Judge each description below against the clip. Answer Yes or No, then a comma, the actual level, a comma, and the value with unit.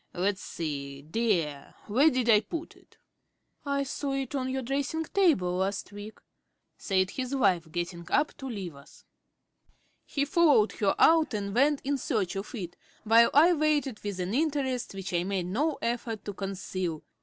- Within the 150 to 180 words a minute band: Yes, average, 165 wpm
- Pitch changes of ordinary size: No, wide, 6.8 semitones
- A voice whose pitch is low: No, high, 220 Hz